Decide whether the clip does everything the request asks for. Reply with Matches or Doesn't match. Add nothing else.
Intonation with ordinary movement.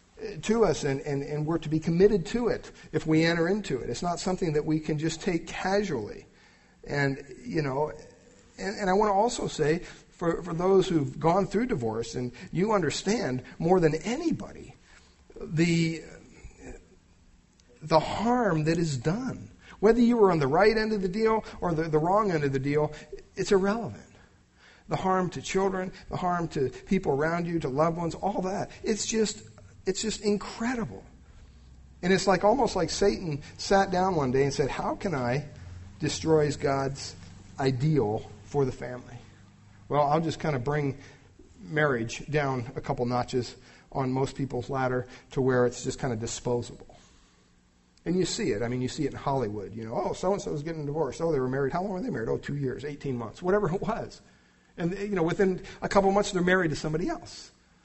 Doesn't match